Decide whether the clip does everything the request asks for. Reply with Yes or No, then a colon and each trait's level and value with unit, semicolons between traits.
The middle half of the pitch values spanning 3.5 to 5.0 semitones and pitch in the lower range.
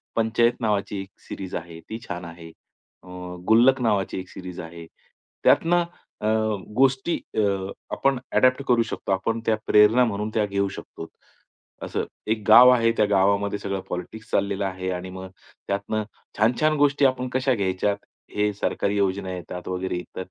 Yes: average, 3.9 semitones; low, 100 Hz